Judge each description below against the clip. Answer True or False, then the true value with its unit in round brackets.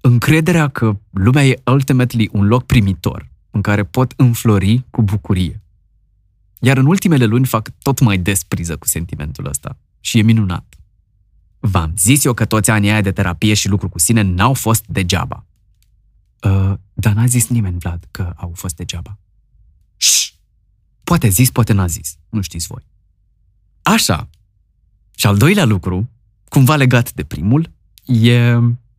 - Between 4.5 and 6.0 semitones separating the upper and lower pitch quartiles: False (3.9 semitones)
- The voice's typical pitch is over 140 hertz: False (105 Hz)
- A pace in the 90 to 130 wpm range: False (150 wpm)